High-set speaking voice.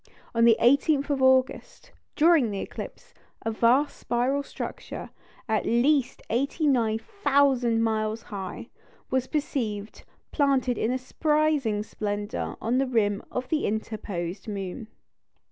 Yes: high, 240 Hz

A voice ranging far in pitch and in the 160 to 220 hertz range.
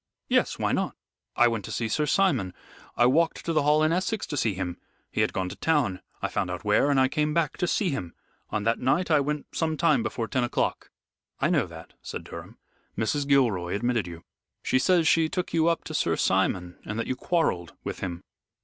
No: wide, 7.1 semitones; low, 135 Hz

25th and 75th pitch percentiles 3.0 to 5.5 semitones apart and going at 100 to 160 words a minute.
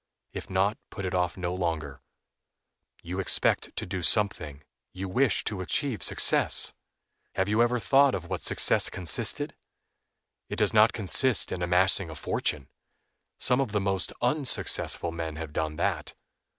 Yes: average, 4.0 semitones; average, 150 wpm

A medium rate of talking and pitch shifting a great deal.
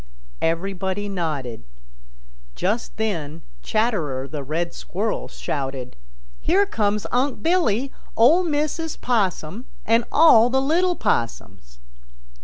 No: slow, 100 wpm; wide, 8.7 semitones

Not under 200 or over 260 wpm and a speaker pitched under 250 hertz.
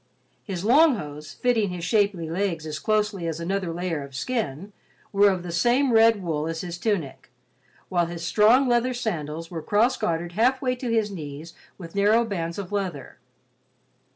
No: average, 170 wpm; high, 190 Hz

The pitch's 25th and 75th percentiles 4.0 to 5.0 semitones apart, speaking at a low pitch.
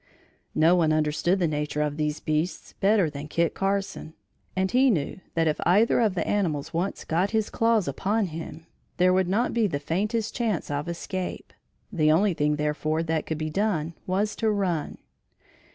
No: average, 4.6 semitones; medium, 170 Hz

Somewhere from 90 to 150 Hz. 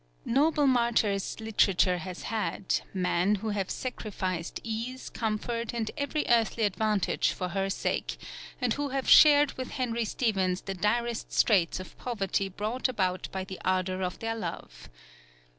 No: high, 215 Hz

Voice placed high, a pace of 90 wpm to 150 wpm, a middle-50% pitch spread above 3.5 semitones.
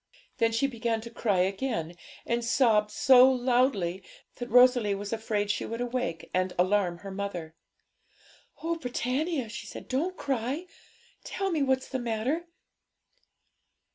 Yes: high, 235 Hz; average, 140 wpm; average, 4.2 semitones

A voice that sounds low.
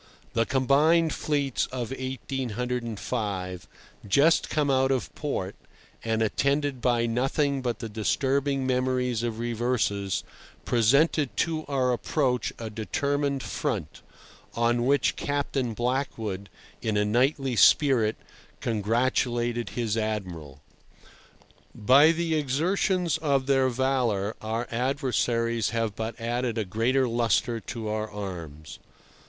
Yes: low, 120 Hz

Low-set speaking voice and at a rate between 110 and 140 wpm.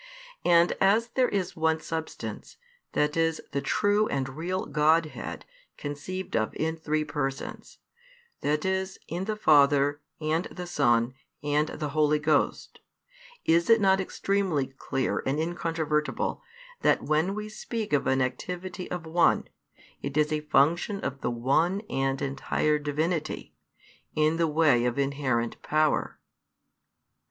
No: medium, 155 Hz; slow, 135 wpm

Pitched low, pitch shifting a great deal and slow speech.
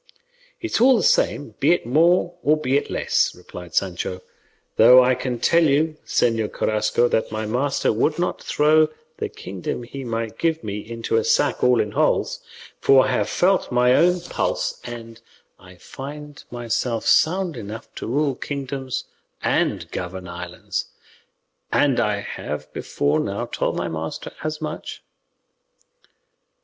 No: low, 125 Hz; wide, 6.0 semitones; average, 150 wpm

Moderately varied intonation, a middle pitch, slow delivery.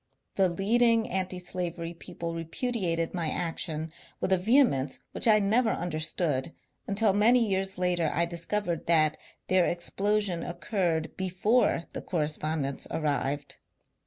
Yes: average, 3.8 semitones; medium, 175 Hz; slow, 125 wpm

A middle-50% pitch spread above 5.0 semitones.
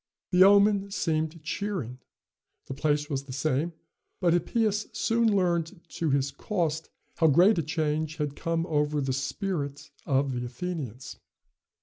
No: average, 4.3 semitones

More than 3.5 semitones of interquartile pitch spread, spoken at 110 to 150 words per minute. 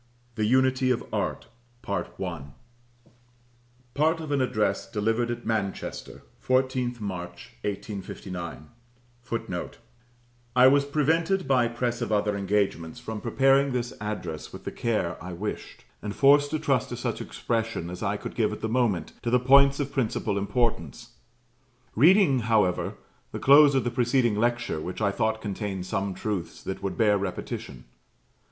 Yes: average, 4.2 semitones; average, 145 wpm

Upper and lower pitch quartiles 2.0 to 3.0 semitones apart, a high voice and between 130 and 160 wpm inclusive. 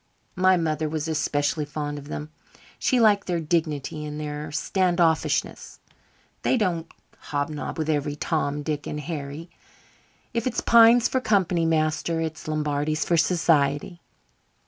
No: narrow, 2.6 semitones; medium, 155 Hz; average, 140 wpm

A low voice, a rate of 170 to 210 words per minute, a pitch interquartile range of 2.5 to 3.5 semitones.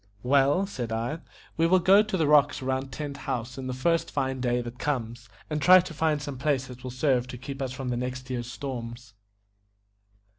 Yes: low, 130 Hz; average, 200 wpm; average, 3.2 semitones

